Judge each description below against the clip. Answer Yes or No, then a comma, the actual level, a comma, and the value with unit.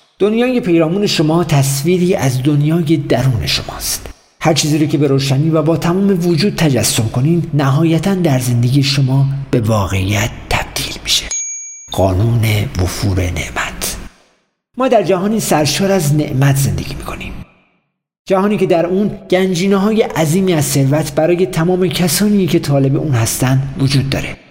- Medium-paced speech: Yes, average, 140 wpm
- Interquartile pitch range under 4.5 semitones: No, average, 5.3 semitones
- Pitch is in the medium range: Yes, medium, 155 Hz